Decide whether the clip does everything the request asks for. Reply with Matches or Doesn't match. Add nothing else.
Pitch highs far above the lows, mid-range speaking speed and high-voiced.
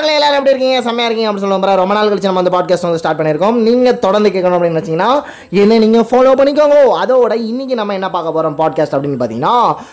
Doesn't match